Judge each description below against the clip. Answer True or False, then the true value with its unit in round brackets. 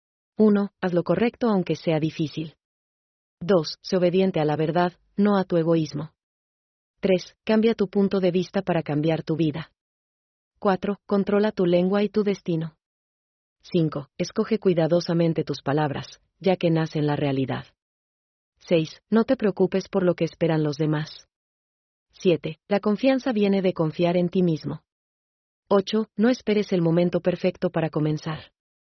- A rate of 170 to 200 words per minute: False (145 wpm)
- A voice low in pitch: False (175 Hz)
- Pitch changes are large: False (4.0 semitones)